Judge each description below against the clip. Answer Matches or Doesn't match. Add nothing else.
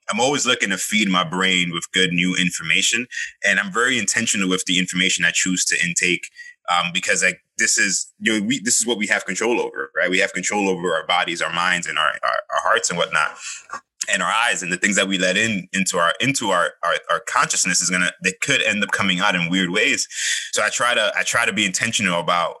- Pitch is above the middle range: Doesn't match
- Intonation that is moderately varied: Doesn't match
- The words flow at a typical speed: Doesn't match